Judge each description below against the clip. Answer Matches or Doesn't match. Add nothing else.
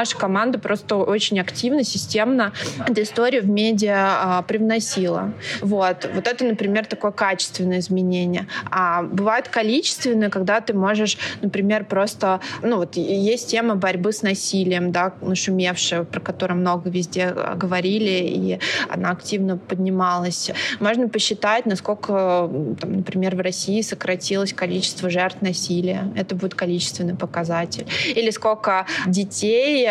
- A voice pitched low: Doesn't match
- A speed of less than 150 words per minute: Matches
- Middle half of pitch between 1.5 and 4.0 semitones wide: Matches